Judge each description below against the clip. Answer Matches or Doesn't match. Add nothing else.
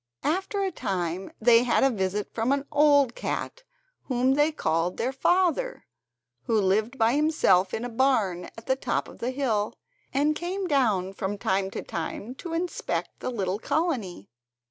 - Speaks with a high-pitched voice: Matches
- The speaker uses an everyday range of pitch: Doesn't match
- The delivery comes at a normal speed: Matches